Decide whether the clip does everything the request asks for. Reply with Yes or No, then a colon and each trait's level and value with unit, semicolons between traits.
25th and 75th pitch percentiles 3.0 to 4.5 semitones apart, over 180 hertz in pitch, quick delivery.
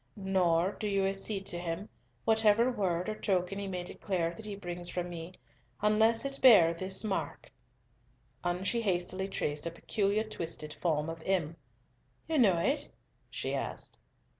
No: average, 3.5 semitones; high, 190 Hz; average, 160 wpm